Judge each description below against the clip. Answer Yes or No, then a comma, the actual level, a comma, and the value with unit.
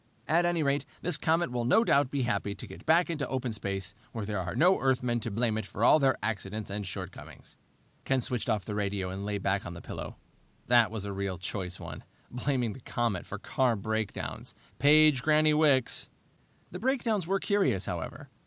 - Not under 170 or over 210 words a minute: Yes, average, 200 wpm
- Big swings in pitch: Yes, wide, 6.6 semitones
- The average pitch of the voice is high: No, low, 120 Hz